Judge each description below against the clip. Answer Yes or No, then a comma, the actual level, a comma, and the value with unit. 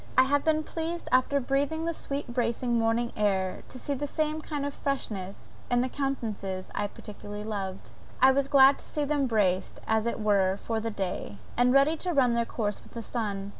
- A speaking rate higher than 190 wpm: Yes, fast, 205 wpm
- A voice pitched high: Yes, high, 245 Hz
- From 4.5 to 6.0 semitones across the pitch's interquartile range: Yes, average, 5.2 semitones